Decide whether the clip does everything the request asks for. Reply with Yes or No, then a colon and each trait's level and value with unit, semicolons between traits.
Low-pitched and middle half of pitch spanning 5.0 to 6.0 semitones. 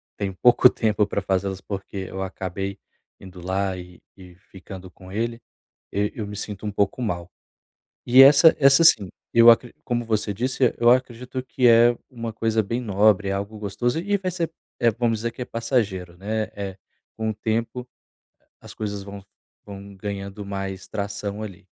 No: low, 105 Hz; average, 3.3 semitones